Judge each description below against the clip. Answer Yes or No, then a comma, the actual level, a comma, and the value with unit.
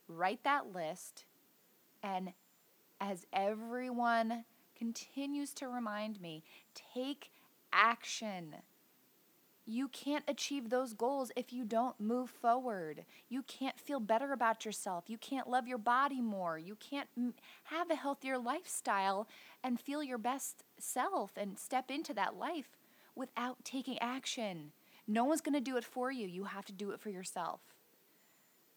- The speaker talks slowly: No, average, 145 wpm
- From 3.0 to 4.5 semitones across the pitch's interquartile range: Yes, average, 3.9 semitones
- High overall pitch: Yes, high, 245 Hz